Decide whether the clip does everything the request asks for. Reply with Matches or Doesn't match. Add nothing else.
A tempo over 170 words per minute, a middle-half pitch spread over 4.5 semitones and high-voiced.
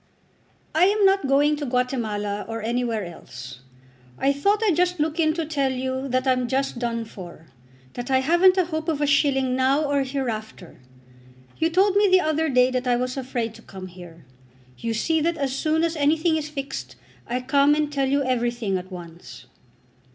Matches